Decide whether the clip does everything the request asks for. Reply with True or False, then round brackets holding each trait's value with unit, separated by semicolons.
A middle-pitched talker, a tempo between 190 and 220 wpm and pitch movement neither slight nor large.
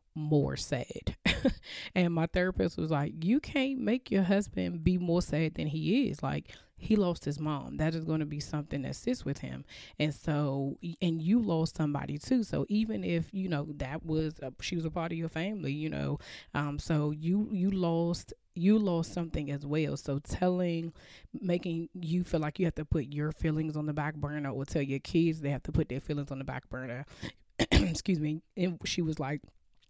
True (160 Hz; 205 wpm; 3.4 semitones)